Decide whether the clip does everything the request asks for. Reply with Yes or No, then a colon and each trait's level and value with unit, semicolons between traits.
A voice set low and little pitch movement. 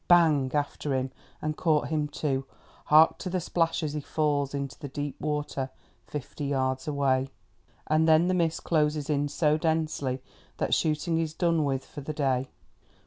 No: medium, 150 Hz; narrow, 2.3 semitones